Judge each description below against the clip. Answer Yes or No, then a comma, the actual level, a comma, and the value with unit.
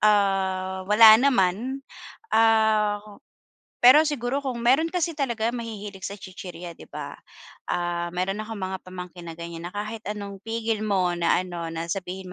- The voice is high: Yes, high, 205 Hz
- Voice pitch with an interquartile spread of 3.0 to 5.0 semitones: Yes, average, 3.8 semitones